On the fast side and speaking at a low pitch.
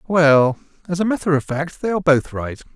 No: fast, 220 wpm; medium, 160 Hz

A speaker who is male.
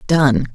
No: female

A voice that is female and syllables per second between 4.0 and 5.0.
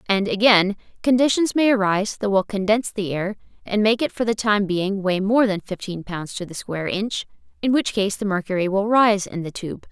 No: female; 5.4 syllables/s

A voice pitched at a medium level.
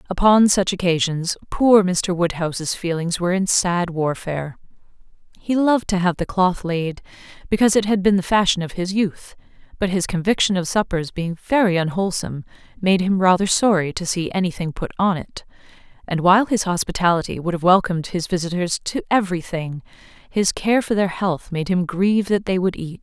Yes: medium, 180 Hz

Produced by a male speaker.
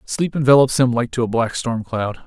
Yes: male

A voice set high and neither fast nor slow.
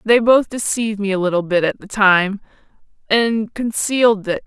Yes: high, 210 Hz; average, 175 wpm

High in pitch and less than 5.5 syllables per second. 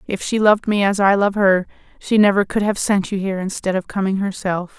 No: high, 195 Hz; 5.8 syllables/s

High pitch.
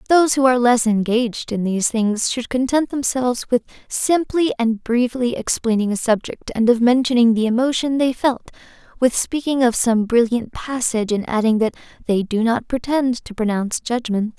Yes: high, 240 Hz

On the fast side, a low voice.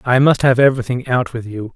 Yes: fast, 240 wpm; low, 125 Hz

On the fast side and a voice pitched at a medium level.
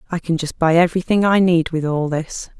Yes: fast, 230 wpm; medium, 170 Hz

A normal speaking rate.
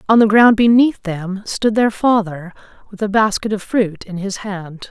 Yes: average, 195 wpm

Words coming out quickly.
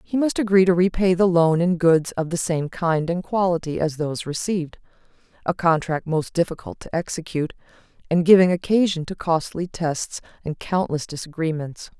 No: average, 165 wpm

